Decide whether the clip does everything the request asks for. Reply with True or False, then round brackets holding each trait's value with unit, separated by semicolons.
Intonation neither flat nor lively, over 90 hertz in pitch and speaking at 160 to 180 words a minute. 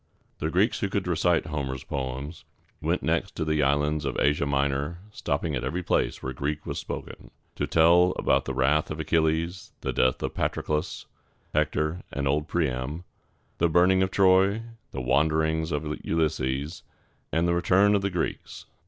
False (3.5 semitones; 80 Hz; 170 wpm)